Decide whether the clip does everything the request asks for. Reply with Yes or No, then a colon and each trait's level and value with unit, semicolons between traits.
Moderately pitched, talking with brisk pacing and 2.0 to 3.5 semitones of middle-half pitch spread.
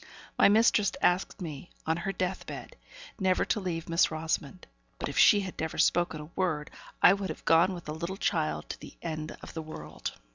Yes: medium, 170 Hz; fast, 210 wpm; average, 3.2 semitones